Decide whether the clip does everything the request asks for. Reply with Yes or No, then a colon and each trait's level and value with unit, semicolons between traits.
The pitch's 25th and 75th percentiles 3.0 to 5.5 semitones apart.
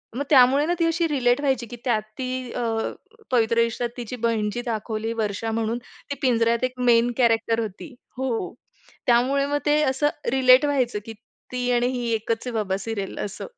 No: narrow, 2.4 semitones